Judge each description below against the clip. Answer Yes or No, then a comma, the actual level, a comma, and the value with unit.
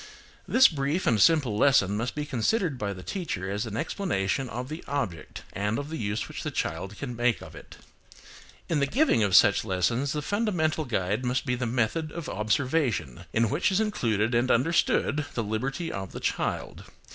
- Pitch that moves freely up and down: Yes, wide, 6.4 semitones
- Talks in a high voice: No, low, 125 Hz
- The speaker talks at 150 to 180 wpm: No, average, 190 wpm